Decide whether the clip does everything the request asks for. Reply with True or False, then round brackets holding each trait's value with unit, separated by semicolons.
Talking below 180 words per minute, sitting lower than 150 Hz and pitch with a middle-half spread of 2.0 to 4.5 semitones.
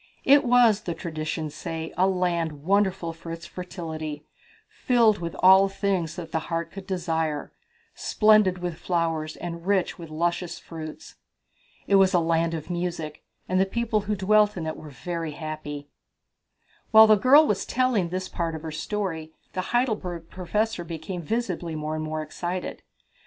False (160 wpm; 175 Hz; 3.4 semitones)